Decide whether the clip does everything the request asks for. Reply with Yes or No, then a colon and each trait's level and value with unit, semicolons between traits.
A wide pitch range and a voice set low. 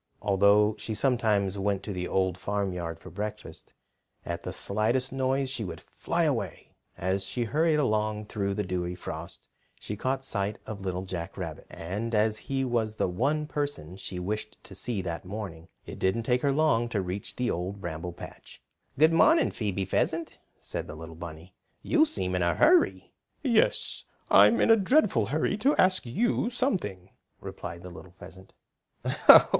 Yes: wide, 6.3 semitones; low, 105 Hz